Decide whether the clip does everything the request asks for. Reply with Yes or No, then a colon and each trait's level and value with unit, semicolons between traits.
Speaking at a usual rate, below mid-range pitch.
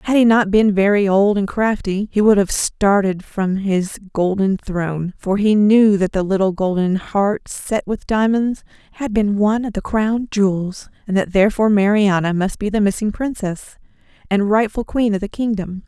No: average, 185 wpm; high, 205 Hz